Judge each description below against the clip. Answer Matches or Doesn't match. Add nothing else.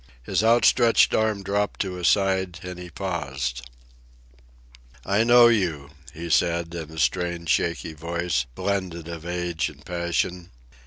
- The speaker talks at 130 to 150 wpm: Matches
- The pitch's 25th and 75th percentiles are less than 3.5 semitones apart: Matches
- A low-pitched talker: Matches